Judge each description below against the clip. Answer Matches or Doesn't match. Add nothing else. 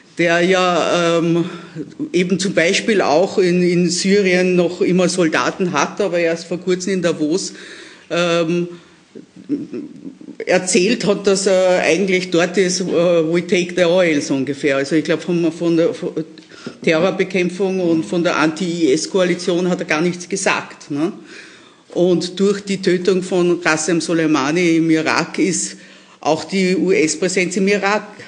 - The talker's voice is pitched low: Doesn't match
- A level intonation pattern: Matches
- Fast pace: Doesn't match